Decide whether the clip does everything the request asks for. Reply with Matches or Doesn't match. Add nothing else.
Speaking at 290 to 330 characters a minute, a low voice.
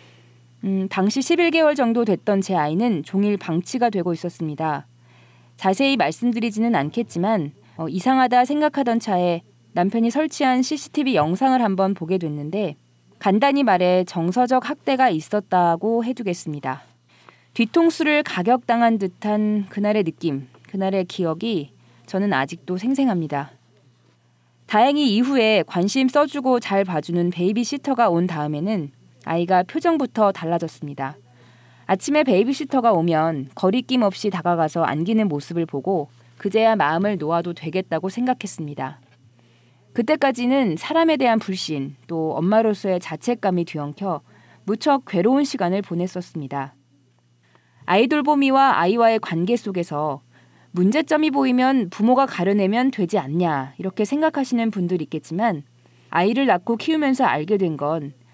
Doesn't match